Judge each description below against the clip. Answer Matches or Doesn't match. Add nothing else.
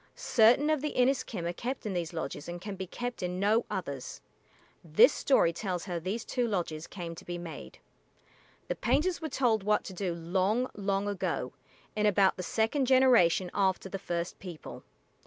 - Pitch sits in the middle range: Doesn't match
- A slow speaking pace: Doesn't match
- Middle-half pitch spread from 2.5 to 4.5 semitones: Doesn't match